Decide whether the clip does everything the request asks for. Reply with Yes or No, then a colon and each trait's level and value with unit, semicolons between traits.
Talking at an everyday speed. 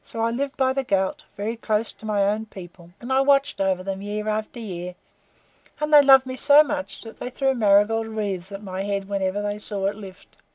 No: fast, 220 wpm